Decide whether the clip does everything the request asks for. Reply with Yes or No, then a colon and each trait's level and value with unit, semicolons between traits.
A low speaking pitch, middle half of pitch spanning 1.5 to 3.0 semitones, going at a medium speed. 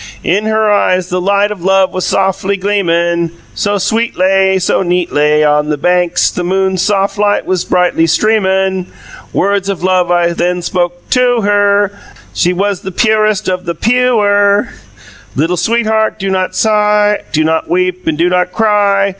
No: high, 190 Hz; narrow, 2.5 semitones; average, 160 wpm